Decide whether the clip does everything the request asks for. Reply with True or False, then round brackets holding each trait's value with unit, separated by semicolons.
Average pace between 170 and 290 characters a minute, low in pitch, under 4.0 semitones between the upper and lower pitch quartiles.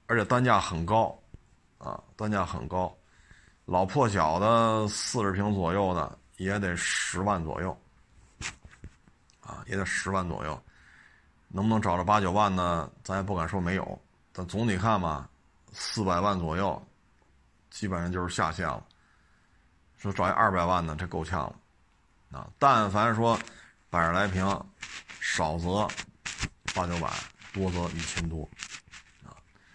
True (195 characters per minute; 95 Hz; 3.5 semitones)